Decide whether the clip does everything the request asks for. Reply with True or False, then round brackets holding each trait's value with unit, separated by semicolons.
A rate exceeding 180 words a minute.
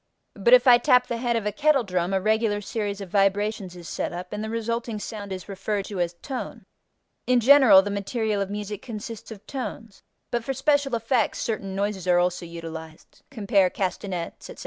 True (195 wpm)